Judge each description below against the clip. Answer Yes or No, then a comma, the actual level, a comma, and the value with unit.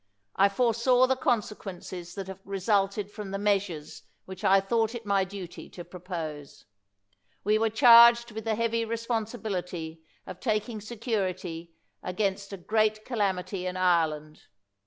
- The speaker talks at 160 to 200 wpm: No, average, 150 wpm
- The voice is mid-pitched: No, high, 200 Hz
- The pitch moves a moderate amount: Yes, average, 3.5 semitones